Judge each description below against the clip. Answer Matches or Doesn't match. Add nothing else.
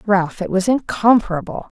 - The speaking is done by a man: Doesn't match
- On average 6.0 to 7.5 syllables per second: Doesn't match